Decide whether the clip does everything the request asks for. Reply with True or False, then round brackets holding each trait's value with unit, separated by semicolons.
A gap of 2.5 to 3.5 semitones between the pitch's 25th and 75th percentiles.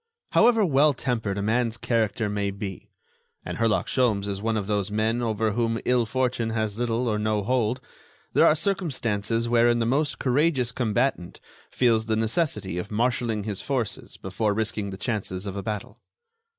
True (2.9 semitones)